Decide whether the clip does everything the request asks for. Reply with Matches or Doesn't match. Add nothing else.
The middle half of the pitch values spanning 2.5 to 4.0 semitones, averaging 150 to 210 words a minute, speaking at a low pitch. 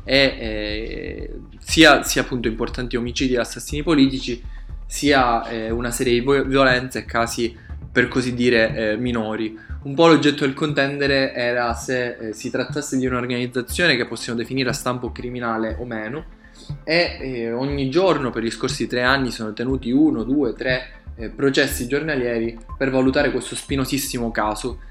Matches